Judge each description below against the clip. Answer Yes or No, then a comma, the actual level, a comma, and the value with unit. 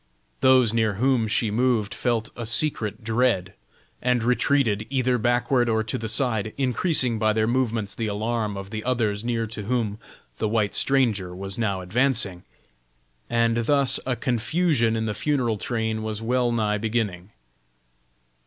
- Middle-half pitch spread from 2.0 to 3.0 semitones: Yes, average, 2.7 semitones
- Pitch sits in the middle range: No, low, 115 Hz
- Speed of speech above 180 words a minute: No, average, 155 wpm